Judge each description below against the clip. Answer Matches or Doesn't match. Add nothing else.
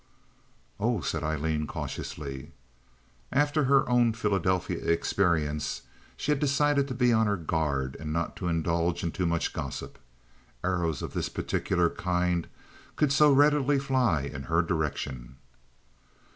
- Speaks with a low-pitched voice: Matches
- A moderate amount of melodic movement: Doesn't match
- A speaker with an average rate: Doesn't match